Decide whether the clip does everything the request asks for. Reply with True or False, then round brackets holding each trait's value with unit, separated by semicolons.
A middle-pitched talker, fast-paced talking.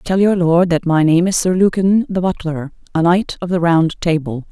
True (175 Hz; 225 wpm)